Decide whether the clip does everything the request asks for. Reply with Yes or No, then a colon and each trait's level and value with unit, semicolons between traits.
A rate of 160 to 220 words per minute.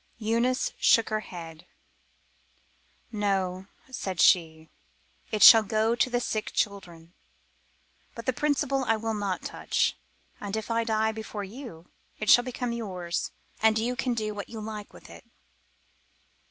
No: average, 145 wpm